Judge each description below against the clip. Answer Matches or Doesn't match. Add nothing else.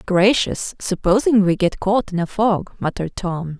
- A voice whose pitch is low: Doesn't match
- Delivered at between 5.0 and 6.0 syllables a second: Doesn't match